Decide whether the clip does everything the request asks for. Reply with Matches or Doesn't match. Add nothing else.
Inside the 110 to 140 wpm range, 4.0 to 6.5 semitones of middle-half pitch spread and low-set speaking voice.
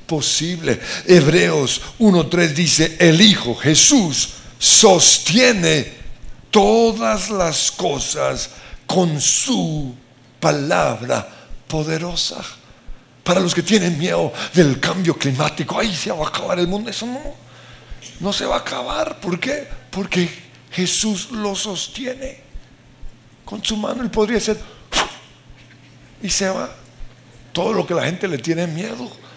Doesn't match